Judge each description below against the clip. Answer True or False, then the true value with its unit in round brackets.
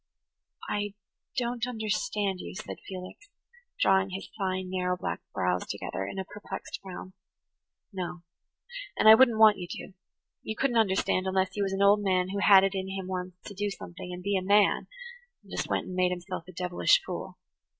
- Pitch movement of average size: False (2.2 semitones)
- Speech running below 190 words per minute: True (180 wpm)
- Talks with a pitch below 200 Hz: True (190 Hz)